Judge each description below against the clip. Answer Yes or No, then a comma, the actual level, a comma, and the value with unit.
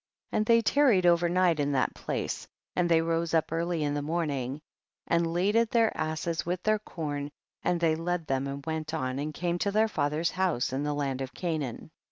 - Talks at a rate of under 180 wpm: No, fast, 205 wpm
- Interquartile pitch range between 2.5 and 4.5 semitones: Yes, average, 3.4 semitones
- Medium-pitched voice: Yes, medium, 165 Hz